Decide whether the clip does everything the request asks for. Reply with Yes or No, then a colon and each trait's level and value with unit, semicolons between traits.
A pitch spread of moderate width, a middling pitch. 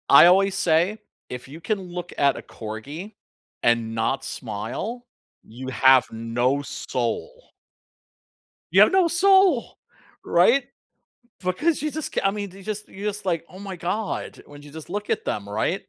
No: wide, 8.4 semitones; medium, 175 Hz